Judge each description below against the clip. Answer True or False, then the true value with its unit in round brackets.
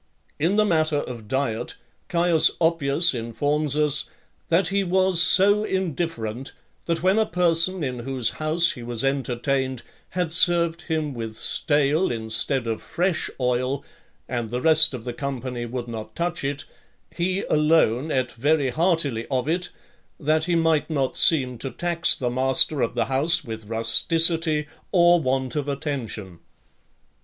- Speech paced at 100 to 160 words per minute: True (150 wpm)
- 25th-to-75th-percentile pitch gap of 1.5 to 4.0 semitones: False (4.9 semitones)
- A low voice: False (145 Hz)